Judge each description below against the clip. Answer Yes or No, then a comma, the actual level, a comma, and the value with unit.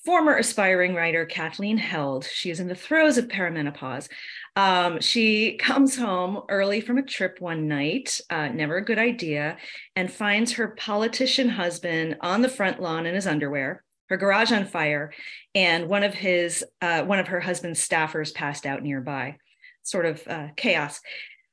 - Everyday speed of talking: Yes, average, 160 wpm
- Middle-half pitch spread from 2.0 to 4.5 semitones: No, average, 5.1 semitones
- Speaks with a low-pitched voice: No, medium, 180 Hz